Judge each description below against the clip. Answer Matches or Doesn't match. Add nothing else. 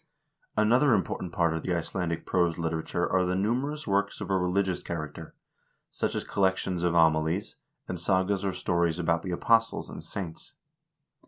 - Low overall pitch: Matches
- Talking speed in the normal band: Matches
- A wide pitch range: Doesn't match